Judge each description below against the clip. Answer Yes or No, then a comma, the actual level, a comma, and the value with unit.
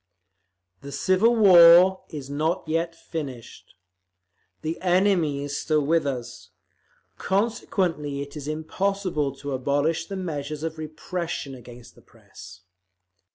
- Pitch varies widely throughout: No, average, 4.2 semitones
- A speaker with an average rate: No, slow, 115 wpm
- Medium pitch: Yes, medium, 155 Hz